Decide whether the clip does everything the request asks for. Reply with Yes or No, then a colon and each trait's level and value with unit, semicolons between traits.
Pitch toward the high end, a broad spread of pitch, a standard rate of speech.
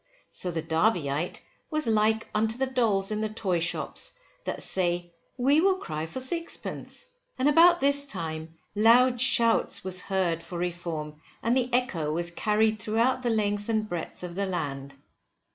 Yes: high, 210 Hz; wide, 6.2 semitones; average, 160 wpm